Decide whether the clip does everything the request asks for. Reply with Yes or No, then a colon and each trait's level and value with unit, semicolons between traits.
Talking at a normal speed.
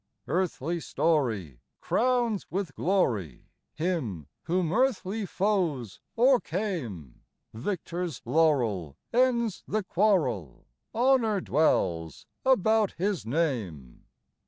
No: slow, 85 wpm